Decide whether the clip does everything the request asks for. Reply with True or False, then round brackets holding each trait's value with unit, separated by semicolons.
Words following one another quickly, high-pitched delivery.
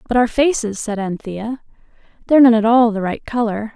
False (190 wpm; 230 Hz)